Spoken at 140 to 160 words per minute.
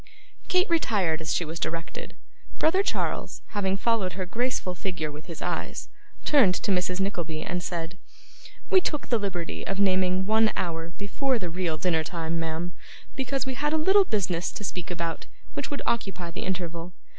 No: average, 175 wpm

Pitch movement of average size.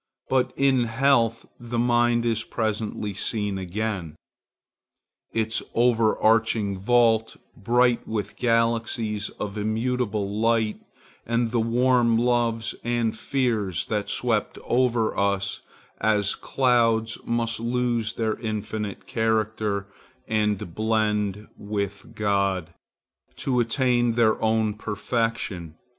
No: narrow, 2.1 semitones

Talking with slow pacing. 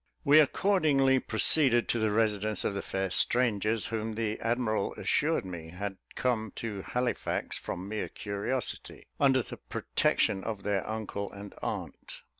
No: average, 145 wpm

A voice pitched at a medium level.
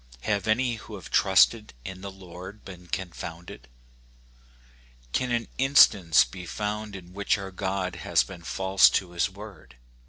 No: very low, 95 Hz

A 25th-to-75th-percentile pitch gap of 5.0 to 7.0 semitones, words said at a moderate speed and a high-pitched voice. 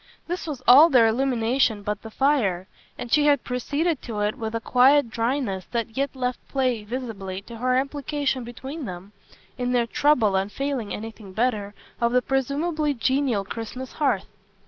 No: average, 3.8 semitones; average, 170 wpm; high, 245 Hz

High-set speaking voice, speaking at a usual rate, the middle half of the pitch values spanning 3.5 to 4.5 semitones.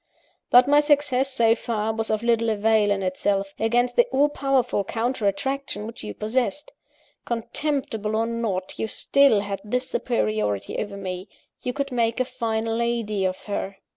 Yes: high, 225 Hz; average, 165 wpm; average, 3.8 semitones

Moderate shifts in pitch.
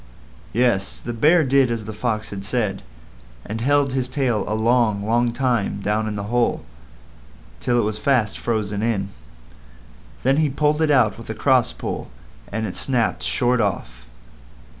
Yes: average, 3.3 semitones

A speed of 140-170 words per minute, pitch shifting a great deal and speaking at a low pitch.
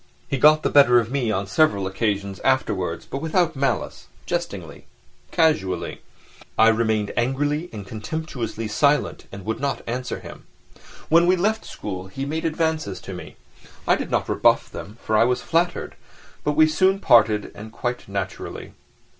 Yes: average, 160 wpm; wide, 6.6 semitones; low, 125 Hz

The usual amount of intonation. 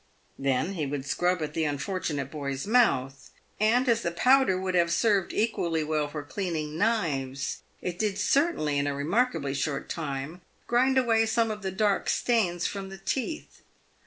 No: wide, 7.1 semitones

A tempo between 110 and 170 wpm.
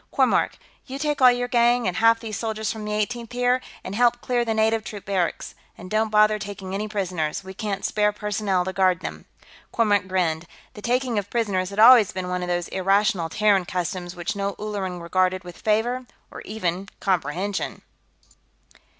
No: average, 185 wpm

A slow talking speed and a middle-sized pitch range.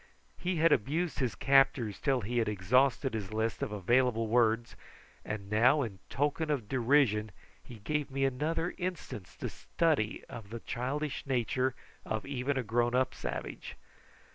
No: average, 155 wpm; average, 4.2 semitones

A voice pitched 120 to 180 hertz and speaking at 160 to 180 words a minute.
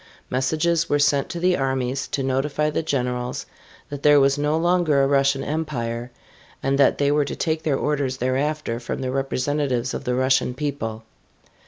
Yes: medium, 140 Hz; average, 175 wpm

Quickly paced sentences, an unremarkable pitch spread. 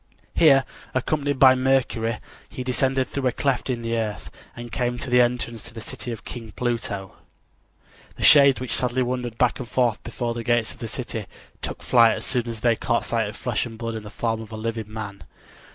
No: fast, 215 wpm; narrow, 2.2 semitones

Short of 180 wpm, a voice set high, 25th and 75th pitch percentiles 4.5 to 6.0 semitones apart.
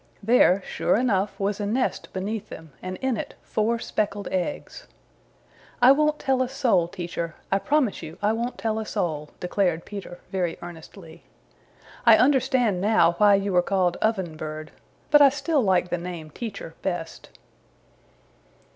Yes: average, 155 wpm; high, 200 Hz; average, 5.1 semitones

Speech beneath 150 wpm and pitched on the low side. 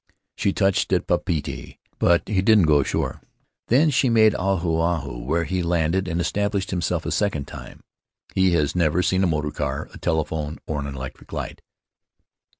No: average, 170 wpm; very low, 85 Hz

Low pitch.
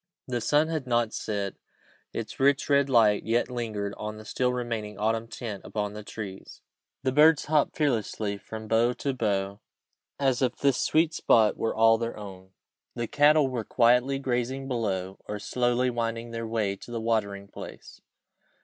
Yes: low, 115 Hz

